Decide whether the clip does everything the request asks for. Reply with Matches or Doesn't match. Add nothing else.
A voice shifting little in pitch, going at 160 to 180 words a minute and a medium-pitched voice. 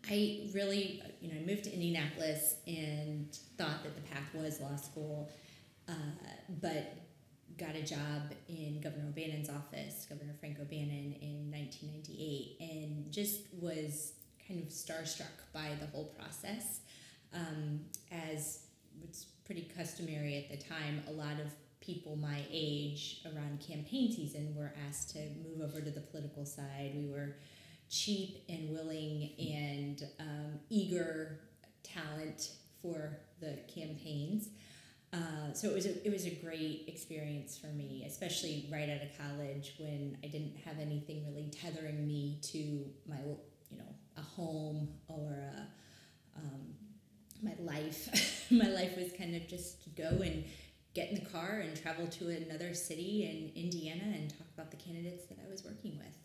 Doesn't match